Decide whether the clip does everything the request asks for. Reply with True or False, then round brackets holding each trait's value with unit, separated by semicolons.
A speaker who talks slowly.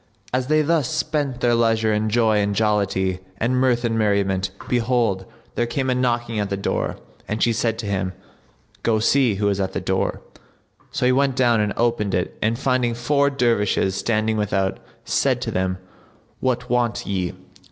False (180 wpm)